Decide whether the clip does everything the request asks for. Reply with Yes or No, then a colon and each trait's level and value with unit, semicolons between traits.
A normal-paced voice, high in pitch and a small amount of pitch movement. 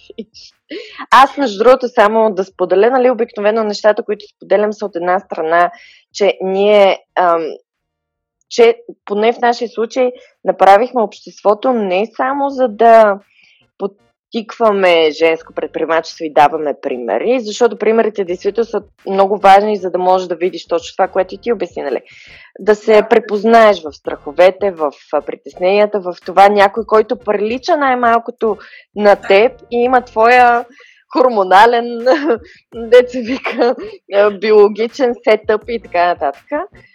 No: average, 125 wpm; high, 210 Hz; average, 4.0 semitones